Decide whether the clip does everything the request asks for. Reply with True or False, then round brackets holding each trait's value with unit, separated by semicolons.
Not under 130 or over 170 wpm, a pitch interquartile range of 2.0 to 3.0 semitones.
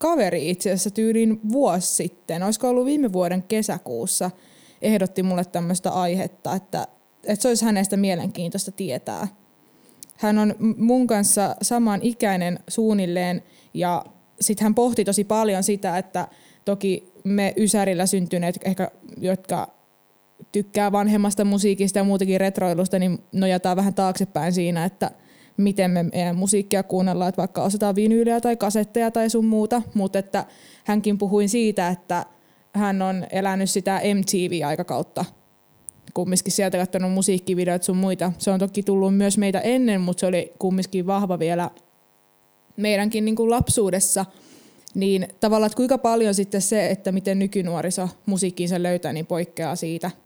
True (140 wpm; 2.4 semitones)